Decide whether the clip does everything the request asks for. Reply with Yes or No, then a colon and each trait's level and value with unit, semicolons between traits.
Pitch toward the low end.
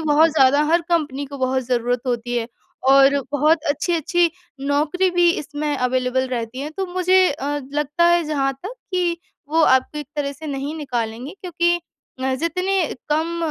No: very high, 295 Hz